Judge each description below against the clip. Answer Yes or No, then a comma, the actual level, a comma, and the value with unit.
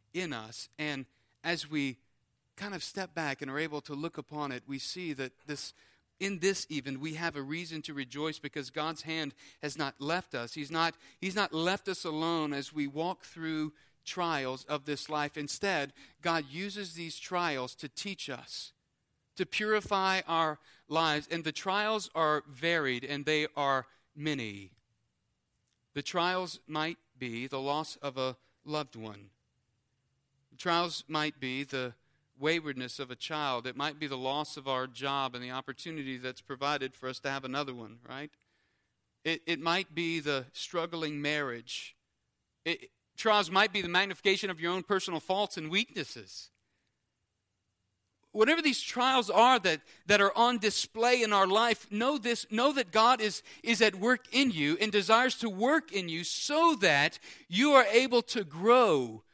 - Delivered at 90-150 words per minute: No, average, 170 wpm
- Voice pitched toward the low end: No, medium, 155 Hz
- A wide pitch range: Yes, wide, 5.8 semitones